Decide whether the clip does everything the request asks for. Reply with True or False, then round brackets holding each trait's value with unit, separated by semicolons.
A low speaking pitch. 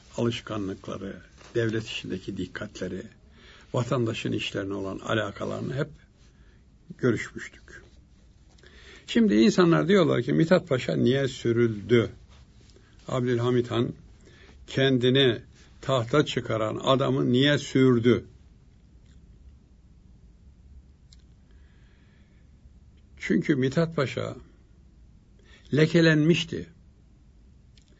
True (120 Hz)